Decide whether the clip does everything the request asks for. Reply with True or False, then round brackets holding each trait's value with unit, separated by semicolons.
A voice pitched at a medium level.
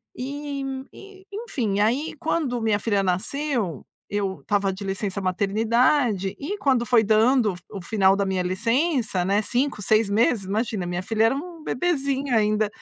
False (220 Hz)